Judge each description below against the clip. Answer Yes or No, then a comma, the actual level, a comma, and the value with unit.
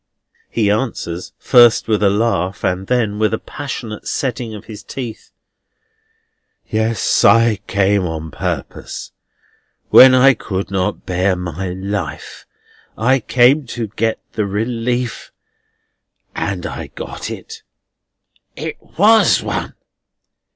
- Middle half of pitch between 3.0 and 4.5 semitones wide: Yes, average, 3.9 semitones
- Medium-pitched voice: No, low, 110 Hz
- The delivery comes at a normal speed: No, slow, 115 wpm